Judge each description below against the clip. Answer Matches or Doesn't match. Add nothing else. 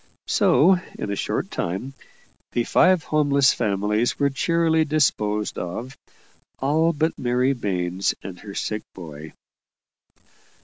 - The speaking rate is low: Matches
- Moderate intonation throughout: Doesn't match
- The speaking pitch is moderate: Doesn't match